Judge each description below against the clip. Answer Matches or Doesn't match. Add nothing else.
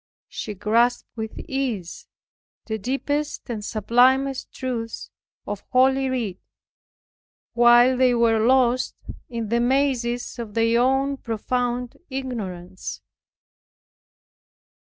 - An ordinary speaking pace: Doesn't match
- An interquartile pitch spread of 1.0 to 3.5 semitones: Matches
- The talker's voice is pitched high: Matches